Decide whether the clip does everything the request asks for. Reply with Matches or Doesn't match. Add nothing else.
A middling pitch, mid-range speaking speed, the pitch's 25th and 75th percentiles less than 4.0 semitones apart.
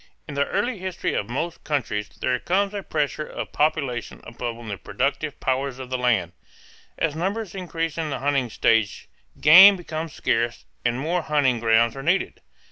Doesn't match